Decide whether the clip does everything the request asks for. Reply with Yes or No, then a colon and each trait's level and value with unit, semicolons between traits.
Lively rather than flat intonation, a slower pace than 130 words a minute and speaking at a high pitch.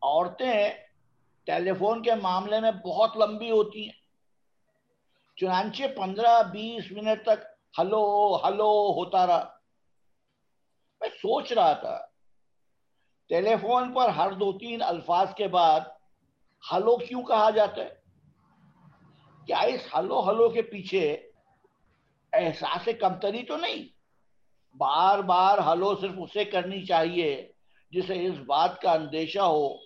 No: average, 3.7 semitones; average, 120 wpm; high, 210 Hz